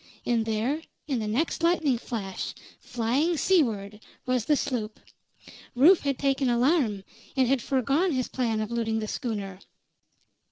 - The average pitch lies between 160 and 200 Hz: No, high, 245 Hz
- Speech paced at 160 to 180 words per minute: No, average, 145 wpm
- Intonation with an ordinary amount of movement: Yes, average, 4.2 semitones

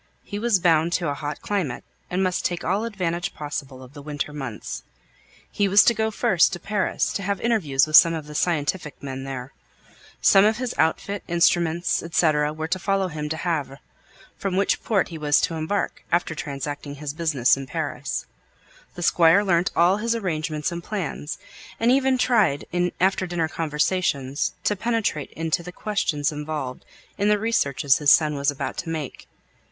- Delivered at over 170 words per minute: Yes, average, 180 wpm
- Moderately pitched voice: Yes, medium, 165 Hz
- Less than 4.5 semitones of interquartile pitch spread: No, average, 4.8 semitones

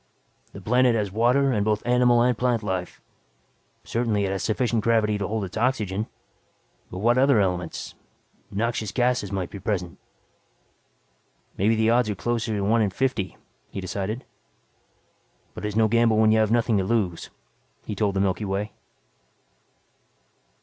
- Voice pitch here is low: Yes, low, 110 Hz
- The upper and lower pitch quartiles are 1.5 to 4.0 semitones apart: Yes, average, 3.0 semitones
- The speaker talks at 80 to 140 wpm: No, average, 155 wpm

